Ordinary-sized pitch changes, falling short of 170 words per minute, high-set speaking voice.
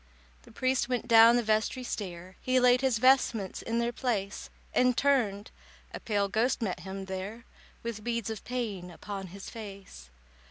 Yes: average, 3.9 semitones; average, 160 wpm; high, 225 Hz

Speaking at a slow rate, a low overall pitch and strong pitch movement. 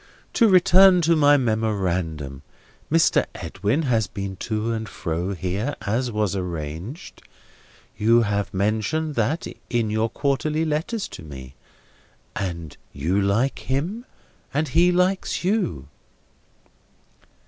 Yes: slow, 115 wpm; low, 110 Hz; wide, 8.5 semitones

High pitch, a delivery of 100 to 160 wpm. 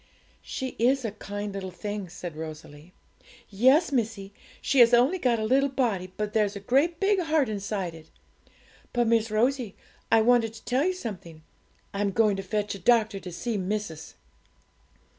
No: high, 215 Hz; average, 170 wpm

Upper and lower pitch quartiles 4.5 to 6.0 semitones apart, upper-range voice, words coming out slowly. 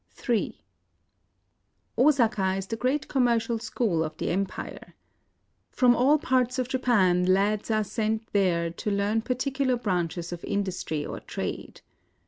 Yes: average, 4.9 semitones; high, 215 Hz; slow, 130 wpm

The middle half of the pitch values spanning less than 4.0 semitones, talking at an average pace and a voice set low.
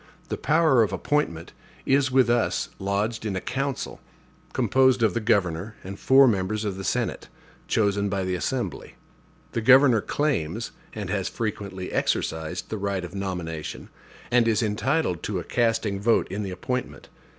No: average, 4.5 semitones; average, 160 wpm; low, 105 Hz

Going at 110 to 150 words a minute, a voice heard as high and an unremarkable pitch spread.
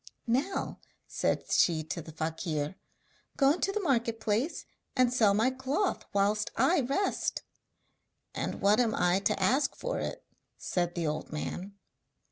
No: average, 145 wpm; high, 220 Hz; wide, 7.2 semitones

